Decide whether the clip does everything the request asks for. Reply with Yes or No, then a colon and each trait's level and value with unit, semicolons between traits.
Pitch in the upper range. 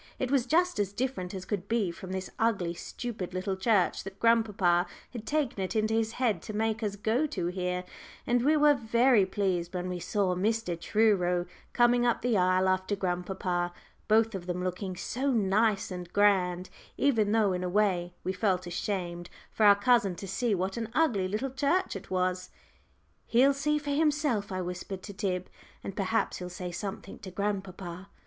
Yes: high, 200 Hz